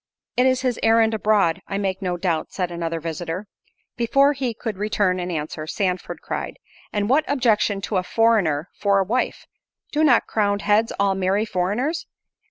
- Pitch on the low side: No, high, 205 Hz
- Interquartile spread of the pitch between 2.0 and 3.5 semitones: No, average, 4.0 semitones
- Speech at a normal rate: Yes, average, 175 wpm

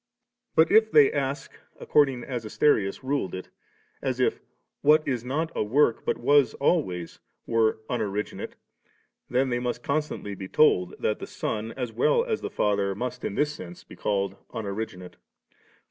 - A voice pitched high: No, low, 125 Hz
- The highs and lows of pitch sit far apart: Yes, wide, 6.0 semitones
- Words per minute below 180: Yes, average, 160 wpm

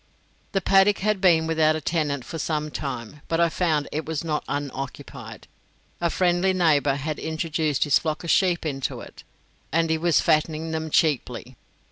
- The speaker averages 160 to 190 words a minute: Yes, average, 170 wpm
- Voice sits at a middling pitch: Yes, medium, 160 Hz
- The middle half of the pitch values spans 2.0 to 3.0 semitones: Yes, narrow, 2.4 semitones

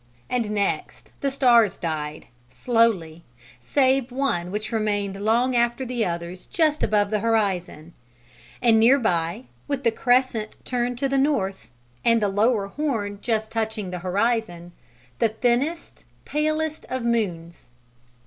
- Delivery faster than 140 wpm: No, slow, 135 wpm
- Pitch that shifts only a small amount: No, average, 4.3 semitones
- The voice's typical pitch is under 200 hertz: No, high, 225 Hz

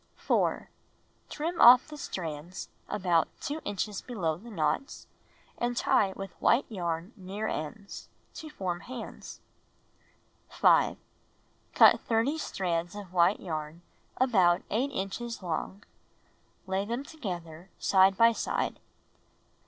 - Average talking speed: No, slow, 120 wpm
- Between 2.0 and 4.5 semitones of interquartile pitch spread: No, average, 5.3 semitones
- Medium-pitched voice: No, high, 195 Hz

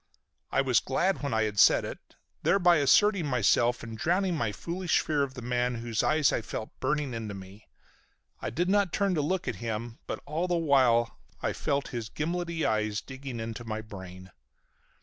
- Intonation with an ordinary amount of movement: No, wide, 6.7 semitones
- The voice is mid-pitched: No, low, 130 Hz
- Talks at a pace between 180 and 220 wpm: Yes, average, 190 wpm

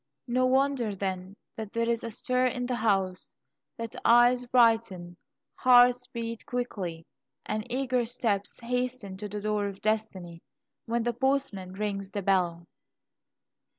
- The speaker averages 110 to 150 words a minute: Yes, average, 140 wpm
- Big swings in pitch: No, average, 3.9 semitones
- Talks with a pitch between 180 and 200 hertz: No, high, 225 Hz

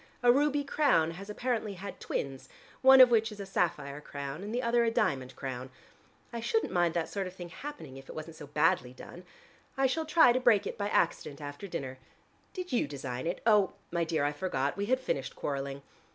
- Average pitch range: No, wide, 8.9 semitones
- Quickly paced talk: Yes, fast, 210 wpm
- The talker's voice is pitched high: No, medium, 180 Hz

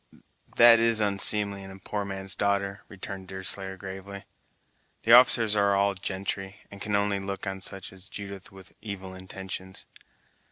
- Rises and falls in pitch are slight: Yes, narrow, 1.0 semitones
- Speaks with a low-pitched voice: Yes, low, 100 Hz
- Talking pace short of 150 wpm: No, average, 155 wpm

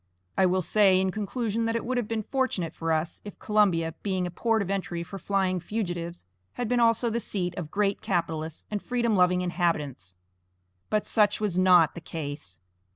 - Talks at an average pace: Yes, average, 190 wpm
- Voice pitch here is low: No, medium, 185 Hz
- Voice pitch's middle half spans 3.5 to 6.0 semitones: Yes, average, 3.9 semitones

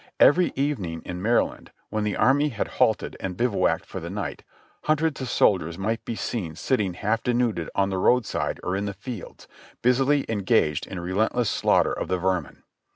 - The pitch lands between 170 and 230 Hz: No, low, 105 Hz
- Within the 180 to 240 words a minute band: Yes, average, 190 wpm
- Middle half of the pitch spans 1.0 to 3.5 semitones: No, average, 5.2 semitones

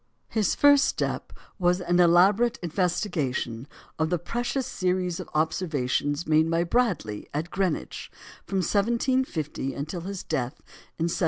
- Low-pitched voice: No, medium, 175 Hz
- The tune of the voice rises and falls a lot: No, average, 4.2 semitones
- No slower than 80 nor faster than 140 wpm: Yes, slow, 135 wpm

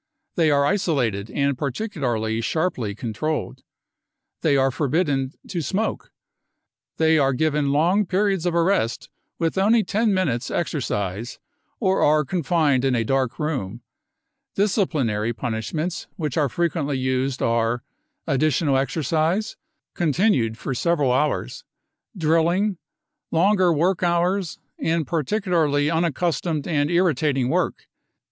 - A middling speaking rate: No, slow, 115 wpm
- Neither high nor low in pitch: Yes, medium, 155 Hz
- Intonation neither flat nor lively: Yes, average, 5.0 semitones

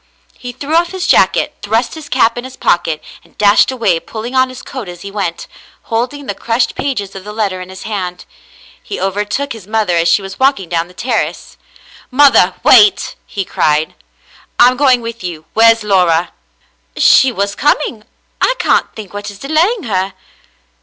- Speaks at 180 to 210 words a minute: Yes, average, 185 wpm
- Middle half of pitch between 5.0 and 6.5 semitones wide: Yes, average, 5.3 semitones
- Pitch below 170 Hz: No, high, 215 Hz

